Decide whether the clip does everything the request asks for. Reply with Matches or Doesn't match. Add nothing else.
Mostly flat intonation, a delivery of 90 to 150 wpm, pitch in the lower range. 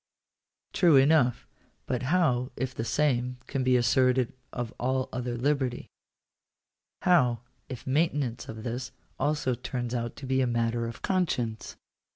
Matches